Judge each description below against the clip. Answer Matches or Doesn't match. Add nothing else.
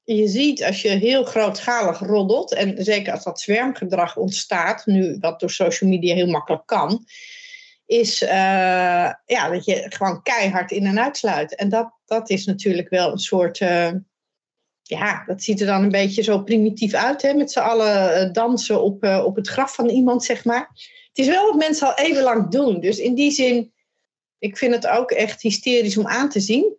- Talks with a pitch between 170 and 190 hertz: Doesn't match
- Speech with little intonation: Doesn't match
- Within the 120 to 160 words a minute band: Doesn't match